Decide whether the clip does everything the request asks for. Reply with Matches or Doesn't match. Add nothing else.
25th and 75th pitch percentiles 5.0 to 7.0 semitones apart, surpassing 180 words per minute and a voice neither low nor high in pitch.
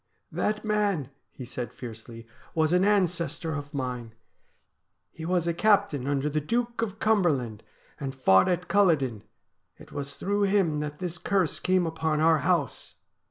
Doesn't match